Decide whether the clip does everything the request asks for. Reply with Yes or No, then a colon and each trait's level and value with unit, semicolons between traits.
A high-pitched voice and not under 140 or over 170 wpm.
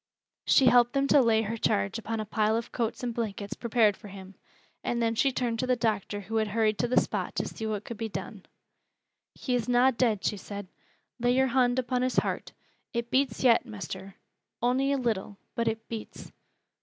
No: high, 230 Hz; fast, 205 wpm